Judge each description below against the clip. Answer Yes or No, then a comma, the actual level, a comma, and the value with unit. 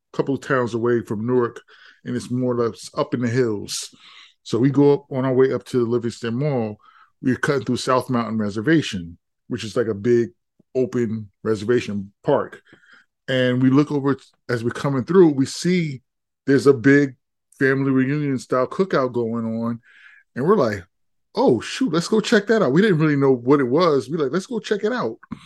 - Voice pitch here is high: No, low, 130 Hz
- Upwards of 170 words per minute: Yes, average, 200 wpm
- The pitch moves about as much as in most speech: Yes, average, 3.4 semitones